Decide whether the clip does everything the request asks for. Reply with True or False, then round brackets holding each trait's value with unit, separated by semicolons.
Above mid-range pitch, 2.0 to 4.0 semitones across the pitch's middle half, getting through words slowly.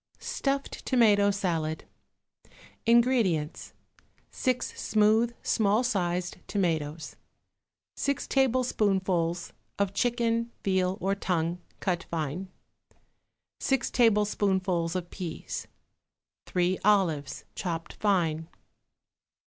False (195 Hz; 4.7 semitones; 80 wpm)